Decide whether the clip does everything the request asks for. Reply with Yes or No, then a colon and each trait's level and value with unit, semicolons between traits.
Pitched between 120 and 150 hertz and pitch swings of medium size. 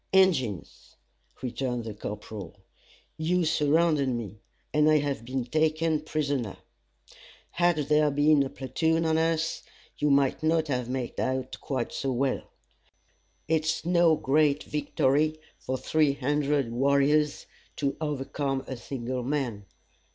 Yes: medium, 140 Hz; average, 3.2 semitones